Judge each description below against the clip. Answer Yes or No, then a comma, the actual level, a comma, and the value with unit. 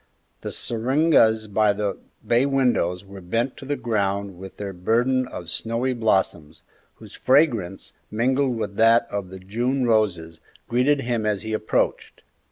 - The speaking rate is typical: Yes, average, 150 wpm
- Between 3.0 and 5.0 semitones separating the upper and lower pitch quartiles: Yes, average, 4.2 semitones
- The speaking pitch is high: No, low, 110 Hz